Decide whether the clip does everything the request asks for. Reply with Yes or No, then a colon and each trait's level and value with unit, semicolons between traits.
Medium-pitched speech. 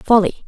No: high, 210 Hz